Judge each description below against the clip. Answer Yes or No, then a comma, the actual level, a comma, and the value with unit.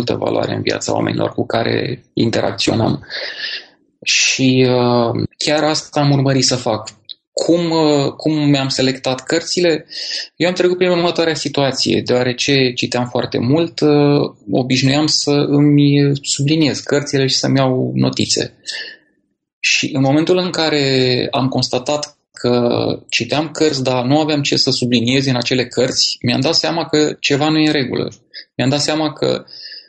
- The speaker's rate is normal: Yes, average, 150 wpm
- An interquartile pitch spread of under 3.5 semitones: Yes, average, 3.1 semitones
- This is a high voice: No, medium, 140 Hz